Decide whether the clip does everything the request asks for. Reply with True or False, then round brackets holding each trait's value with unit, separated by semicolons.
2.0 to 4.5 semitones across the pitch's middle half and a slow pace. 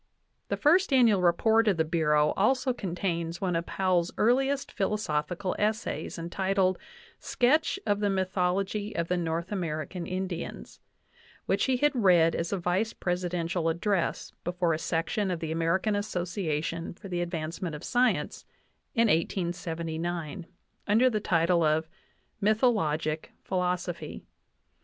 True (3.7 semitones; 130 wpm)